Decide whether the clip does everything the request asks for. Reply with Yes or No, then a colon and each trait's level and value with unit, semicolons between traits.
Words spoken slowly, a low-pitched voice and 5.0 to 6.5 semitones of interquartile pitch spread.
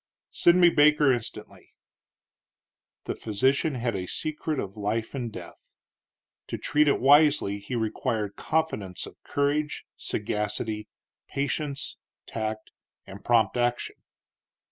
Yes: slow, 115 wpm; low, 120 Hz; wide, 5.6 semitones